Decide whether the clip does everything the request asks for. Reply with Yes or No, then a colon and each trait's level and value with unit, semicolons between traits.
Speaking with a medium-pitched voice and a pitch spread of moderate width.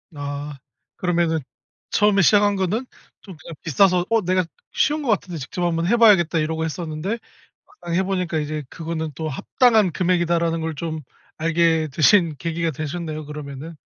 Yes: medium, 170 Hz; average, 3.0 semitones